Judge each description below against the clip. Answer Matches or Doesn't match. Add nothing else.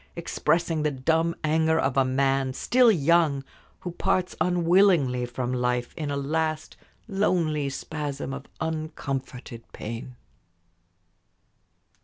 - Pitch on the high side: Doesn't match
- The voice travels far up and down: Doesn't match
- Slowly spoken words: Matches